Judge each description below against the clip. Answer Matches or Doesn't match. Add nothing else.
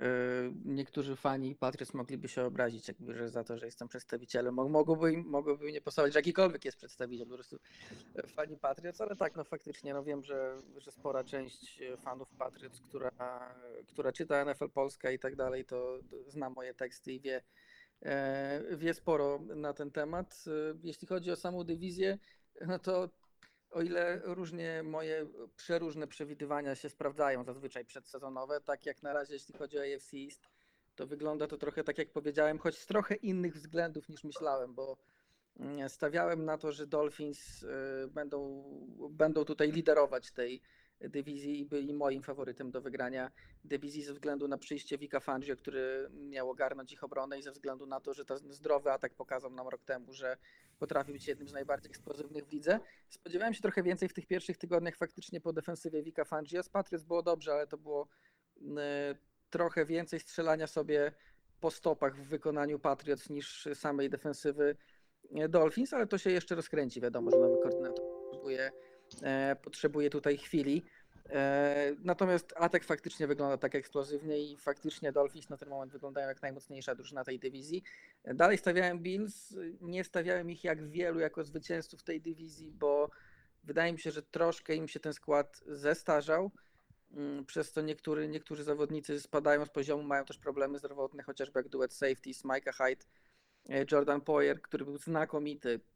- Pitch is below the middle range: Doesn't match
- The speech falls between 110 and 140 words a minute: Doesn't match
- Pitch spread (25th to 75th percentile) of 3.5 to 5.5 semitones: Doesn't match